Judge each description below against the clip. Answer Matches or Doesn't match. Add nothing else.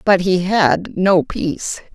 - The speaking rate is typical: Matches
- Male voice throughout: Doesn't match